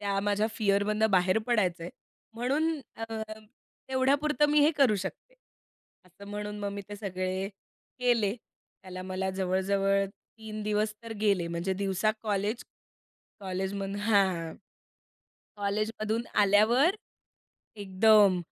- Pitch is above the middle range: Yes, high, 205 Hz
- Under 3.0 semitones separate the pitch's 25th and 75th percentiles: Yes, narrow, 2.4 semitones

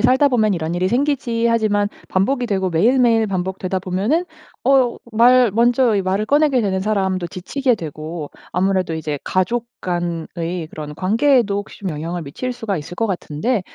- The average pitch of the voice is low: No, high, 200 Hz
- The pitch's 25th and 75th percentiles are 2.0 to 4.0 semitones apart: No, average, 5.2 semitones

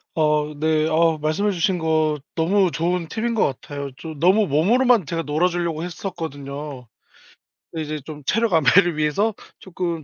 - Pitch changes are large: No, average, 3.1 semitones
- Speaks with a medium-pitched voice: Yes, medium, 160 Hz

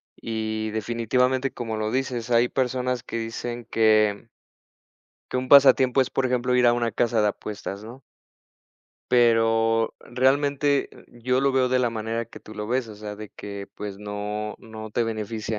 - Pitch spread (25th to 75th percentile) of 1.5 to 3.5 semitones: Yes, narrow, 2.6 semitones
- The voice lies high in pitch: No, low, 115 Hz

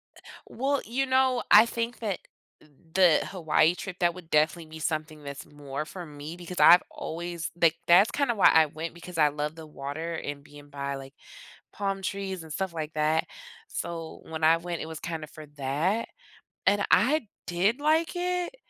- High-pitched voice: No, medium, 170 Hz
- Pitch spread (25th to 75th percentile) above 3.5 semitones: Yes, average, 4.4 semitones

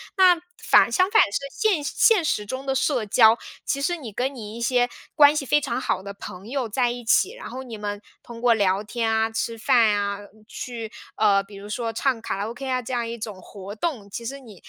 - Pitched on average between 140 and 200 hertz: No, high, 235 Hz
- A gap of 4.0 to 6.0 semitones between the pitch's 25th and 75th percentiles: Yes, average, 4.3 semitones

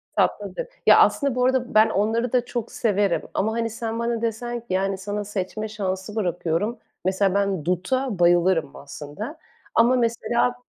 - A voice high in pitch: Yes, high, 215 Hz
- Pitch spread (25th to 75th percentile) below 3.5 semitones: No, average, 3.8 semitones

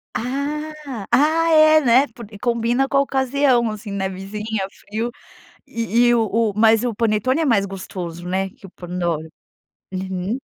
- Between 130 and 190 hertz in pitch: No, high, 225 Hz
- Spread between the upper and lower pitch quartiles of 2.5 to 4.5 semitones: No, average, 5.3 semitones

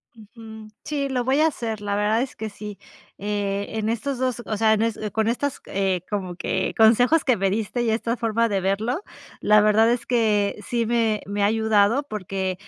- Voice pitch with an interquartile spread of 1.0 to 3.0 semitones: Yes, narrow, 2.5 semitones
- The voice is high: Yes, high, 220 Hz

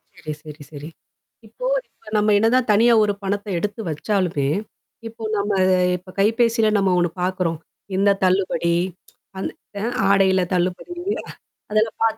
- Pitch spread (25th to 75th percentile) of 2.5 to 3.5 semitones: Yes, average, 3.1 semitones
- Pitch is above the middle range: Yes, high, 195 Hz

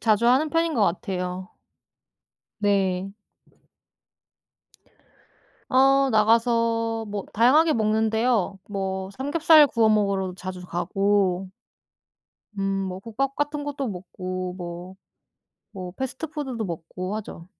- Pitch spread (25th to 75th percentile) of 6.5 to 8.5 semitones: No, average, 5.3 semitones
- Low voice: No, high, 210 Hz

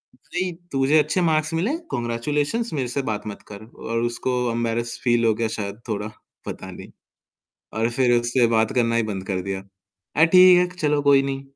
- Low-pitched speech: Yes, low, 120 Hz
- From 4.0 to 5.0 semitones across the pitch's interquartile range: Yes, average, 4.7 semitones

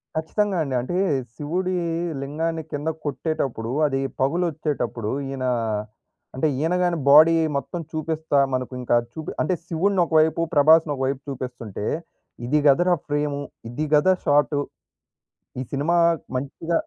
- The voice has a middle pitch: Yes, medium, 150 Hz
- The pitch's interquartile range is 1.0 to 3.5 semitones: Yes, average, 3.1 semitones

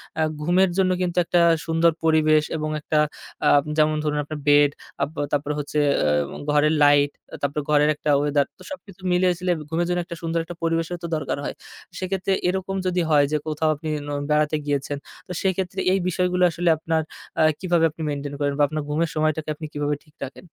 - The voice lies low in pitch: No, medium, 155 Hz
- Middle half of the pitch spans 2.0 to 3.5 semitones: Yes, average, 3.0 semitones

